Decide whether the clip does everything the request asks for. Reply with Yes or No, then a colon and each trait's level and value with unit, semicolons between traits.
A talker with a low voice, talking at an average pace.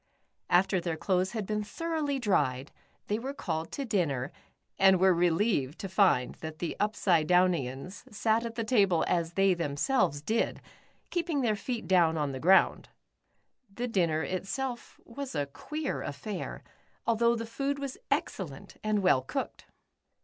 No: high, 195 Hz; average, 150 wpm